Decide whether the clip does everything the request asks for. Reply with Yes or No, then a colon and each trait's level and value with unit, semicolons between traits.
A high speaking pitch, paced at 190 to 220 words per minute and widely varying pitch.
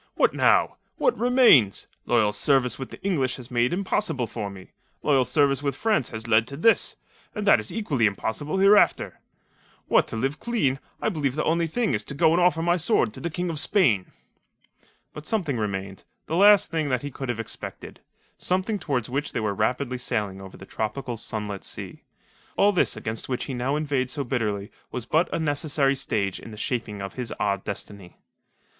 No: low, 135 Hz; average, 195 wpm; wide, 6.9 semitones